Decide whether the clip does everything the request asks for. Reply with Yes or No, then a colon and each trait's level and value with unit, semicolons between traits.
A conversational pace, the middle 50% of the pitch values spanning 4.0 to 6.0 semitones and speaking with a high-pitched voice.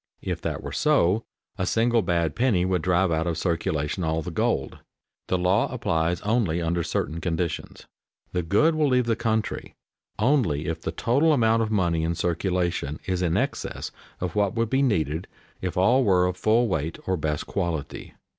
No: average, 180 wpm; average, 5.3 semitones; very low, 90 Hz